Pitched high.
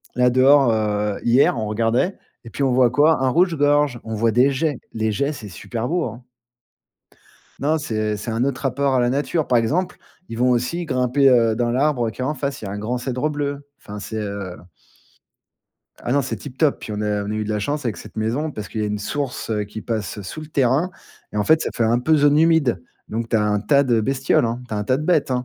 No: low, 125 Hz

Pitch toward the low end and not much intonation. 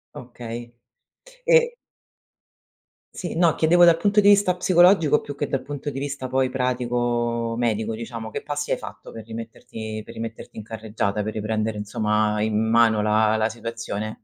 No: low, 115 Hz; average, 4.7 semitones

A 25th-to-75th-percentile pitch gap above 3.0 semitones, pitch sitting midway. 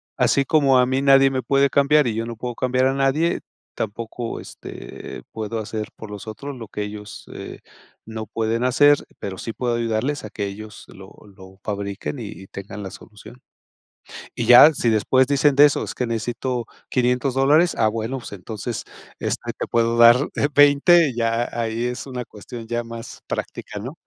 No: average, 3.6 semitones; low, 120 Hz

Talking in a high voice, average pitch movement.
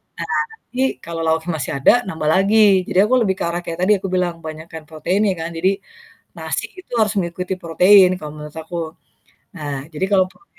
No: medium, 175 Hz; average, 3.1 semitones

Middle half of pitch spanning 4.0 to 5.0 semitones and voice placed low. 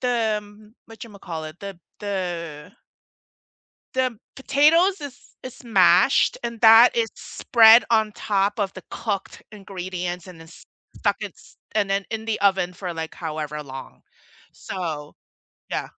No: average, 4.3 semitones; high, 200 Hz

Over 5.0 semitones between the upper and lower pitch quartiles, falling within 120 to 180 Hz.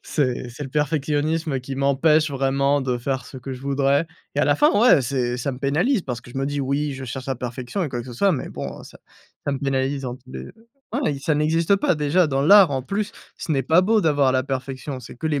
No: average, 2.9 semitones; medium, 140 Hz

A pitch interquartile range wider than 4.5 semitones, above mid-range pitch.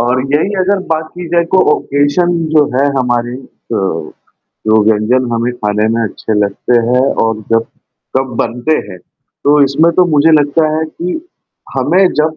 No: wide, 5.4 semitones; low, 135 Hz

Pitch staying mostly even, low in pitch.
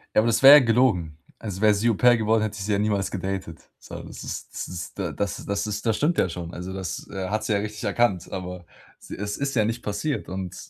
No: average, 3.1 semitones; low, 105 Hz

